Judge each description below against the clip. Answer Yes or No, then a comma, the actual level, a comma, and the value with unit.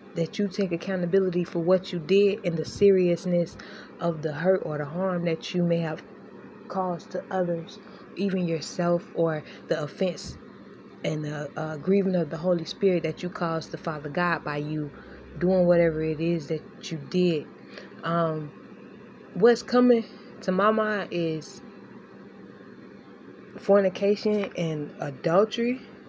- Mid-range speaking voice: Yes, medium, 175 Hz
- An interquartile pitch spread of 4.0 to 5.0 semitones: No, average, 3.3 semitones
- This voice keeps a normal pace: Yes, average, 145 wpm